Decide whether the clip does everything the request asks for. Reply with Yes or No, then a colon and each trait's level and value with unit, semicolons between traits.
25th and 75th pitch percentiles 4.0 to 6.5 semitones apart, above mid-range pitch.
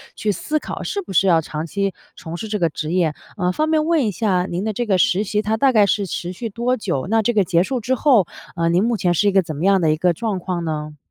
Yes: average, 4.3 semitones; high, 195 Hz